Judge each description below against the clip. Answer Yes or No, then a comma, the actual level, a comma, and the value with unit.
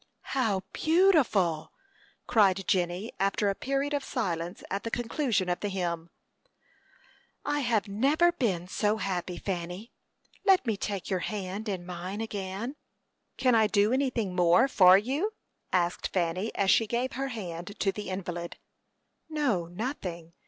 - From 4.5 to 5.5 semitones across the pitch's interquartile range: Yes, average, 5.1 semitones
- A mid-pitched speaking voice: No, high, 200 Hz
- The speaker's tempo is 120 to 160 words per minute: Yes, average, 145 wpm